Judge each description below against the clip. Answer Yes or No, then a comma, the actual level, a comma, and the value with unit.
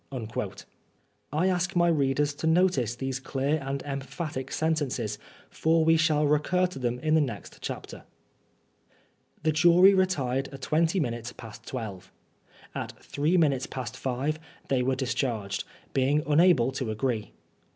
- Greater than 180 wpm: No, average, 140 wpm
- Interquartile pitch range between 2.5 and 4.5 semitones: Yes, average, 4.0 semitones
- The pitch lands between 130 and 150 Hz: Yes, medium, 140 Hz